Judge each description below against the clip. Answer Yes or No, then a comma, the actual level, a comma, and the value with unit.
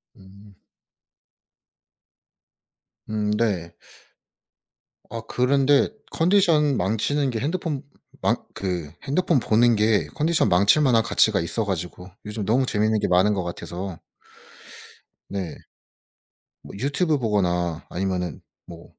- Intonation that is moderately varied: No, wide, 6.5 semitones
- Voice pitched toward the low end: Yes, low, 105 Hz